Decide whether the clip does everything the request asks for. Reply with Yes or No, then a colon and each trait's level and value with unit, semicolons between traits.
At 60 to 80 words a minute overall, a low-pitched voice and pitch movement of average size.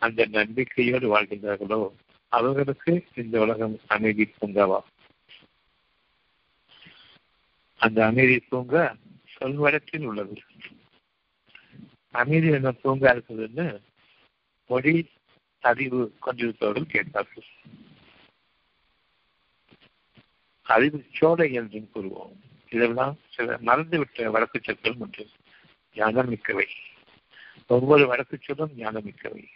Yes: slow, 75 wpm; low, 120 Hz; average, 4.2 semitones